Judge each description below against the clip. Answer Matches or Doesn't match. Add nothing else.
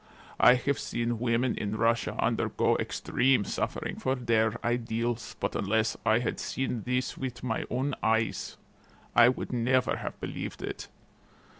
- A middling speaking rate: Matches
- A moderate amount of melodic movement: Doesn't match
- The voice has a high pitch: Doesn't match